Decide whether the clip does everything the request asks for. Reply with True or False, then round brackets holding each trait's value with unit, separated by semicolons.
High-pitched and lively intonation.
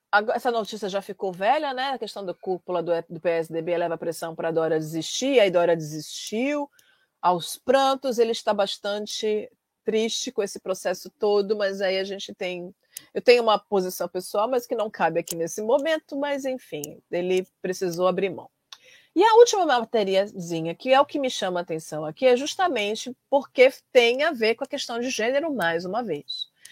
True (205 Hz; 6.4 semitones)